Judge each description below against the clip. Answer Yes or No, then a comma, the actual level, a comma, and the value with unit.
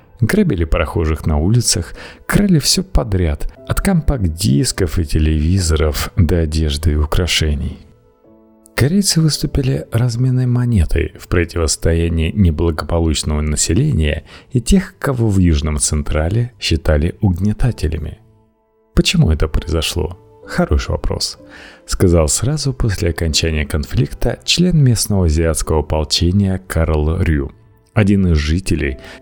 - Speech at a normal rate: No, slow, 105 wpm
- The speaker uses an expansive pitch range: Yes, wide, 5.8 semitones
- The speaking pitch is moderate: No, very low, 90 Hz